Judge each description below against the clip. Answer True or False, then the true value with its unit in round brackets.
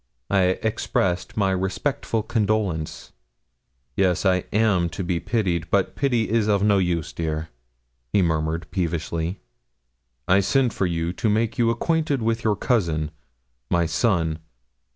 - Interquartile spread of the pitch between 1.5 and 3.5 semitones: False (4.6 semitones)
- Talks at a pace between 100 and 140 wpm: True (135 wpm)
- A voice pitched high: False (95 Hz)